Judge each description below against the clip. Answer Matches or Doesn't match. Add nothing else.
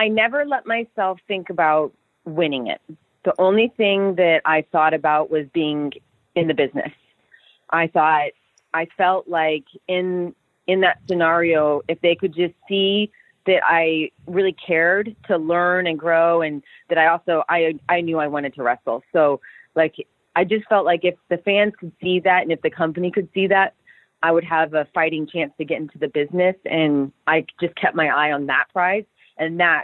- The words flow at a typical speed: Matches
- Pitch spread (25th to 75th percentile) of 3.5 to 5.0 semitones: Doesn't match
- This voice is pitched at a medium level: Matches